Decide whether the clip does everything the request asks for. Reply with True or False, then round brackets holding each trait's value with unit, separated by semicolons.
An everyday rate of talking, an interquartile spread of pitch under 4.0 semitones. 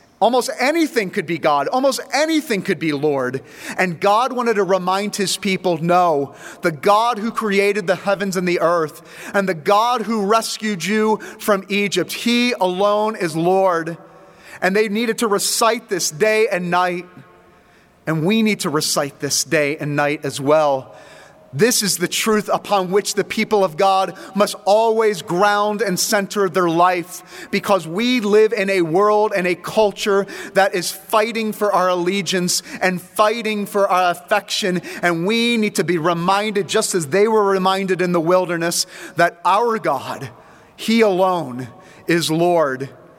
True (165 wpm; 3.3 semitones)